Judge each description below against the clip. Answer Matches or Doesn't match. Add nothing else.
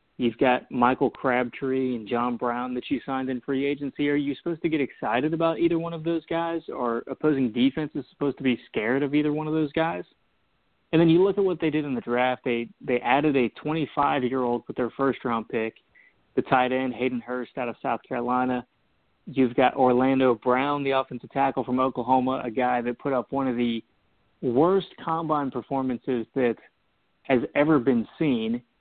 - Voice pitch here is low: Matches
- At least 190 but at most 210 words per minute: Matches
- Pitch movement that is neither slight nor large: Matches